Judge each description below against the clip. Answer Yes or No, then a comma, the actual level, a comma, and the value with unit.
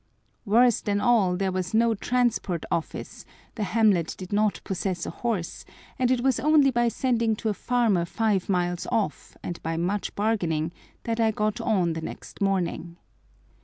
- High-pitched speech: Yes, high, 205 Hz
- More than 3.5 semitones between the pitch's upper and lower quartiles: Yes, average, 4.4 semitones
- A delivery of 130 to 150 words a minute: No, average, 165 wpm